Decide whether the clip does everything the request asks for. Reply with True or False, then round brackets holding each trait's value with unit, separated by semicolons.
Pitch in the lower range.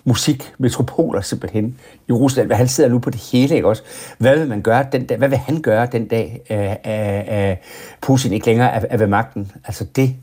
True (120 Hz)